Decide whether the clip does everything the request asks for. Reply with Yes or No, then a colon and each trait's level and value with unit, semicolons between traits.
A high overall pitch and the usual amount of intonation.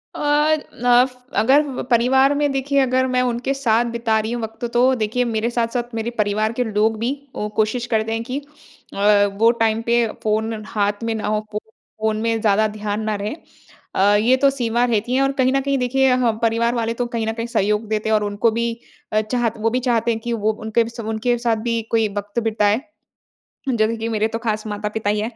No: high, 230 Hz; narrow, 2.0 semitones